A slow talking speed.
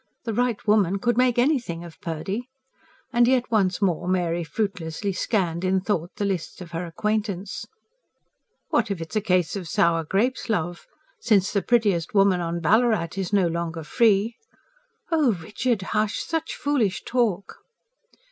No: average, 155 wpm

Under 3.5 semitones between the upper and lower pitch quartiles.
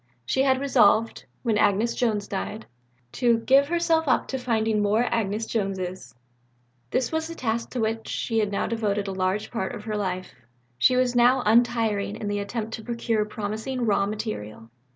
Yes: average, 3.0 semitones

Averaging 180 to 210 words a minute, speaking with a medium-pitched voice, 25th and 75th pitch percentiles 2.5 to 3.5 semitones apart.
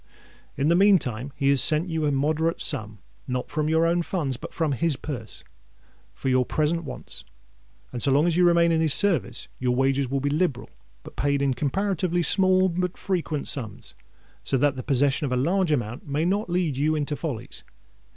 No: average, 190 wpm; medium, 150 Hz; average, 4.1 semitones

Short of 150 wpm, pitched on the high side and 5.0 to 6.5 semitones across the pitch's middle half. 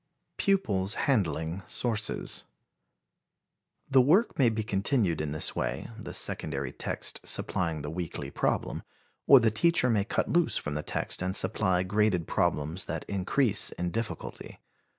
No: average, 140 wpm; low, 100 Hz; wide, 5.5 semitones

